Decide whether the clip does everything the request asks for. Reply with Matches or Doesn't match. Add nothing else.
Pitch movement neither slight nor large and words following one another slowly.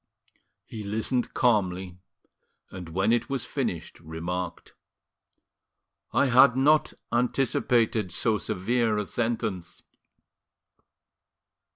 Matches